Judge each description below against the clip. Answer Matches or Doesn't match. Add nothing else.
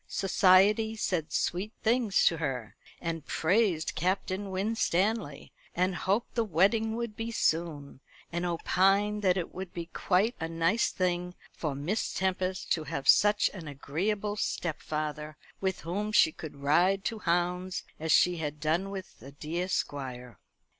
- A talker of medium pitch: Matches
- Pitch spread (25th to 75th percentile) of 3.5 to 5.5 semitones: Matches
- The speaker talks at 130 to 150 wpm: Matches